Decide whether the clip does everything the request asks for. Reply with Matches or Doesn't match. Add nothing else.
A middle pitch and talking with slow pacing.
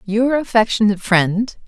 Doesn't match